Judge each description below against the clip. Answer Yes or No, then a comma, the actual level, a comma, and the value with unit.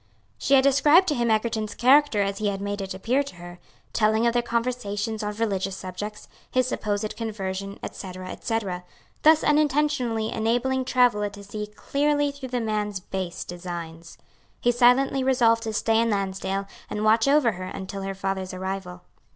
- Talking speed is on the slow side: No, average, 165 wpm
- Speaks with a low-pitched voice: No, high, 215 Hz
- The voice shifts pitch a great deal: No, average, 4.2 semitones